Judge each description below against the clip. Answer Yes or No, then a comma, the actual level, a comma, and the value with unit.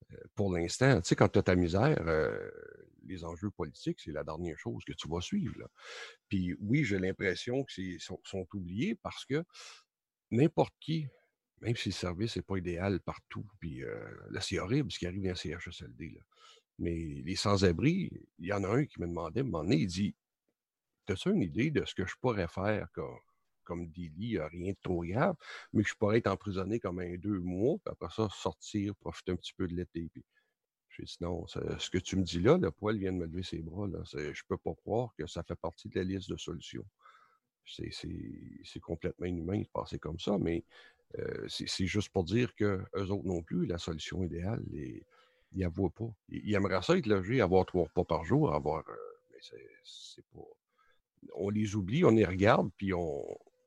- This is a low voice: Yes, very low, 95 Hz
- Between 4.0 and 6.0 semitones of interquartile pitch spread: Yes, average, 4.5 semitones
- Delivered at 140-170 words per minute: No, average, 215 wpm